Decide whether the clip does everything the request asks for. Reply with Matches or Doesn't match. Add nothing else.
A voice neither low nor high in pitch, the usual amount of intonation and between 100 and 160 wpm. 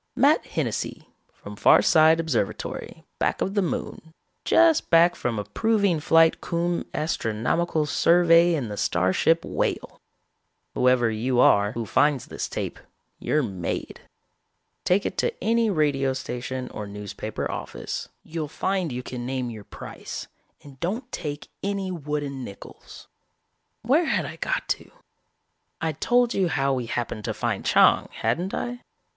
Doesn't match